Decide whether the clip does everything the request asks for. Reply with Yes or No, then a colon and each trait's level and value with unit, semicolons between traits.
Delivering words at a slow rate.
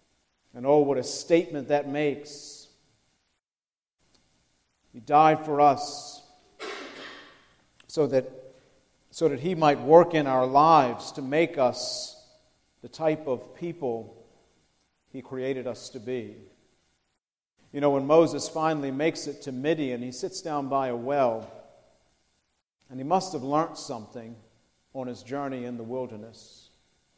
Yes: slow, 130 wpm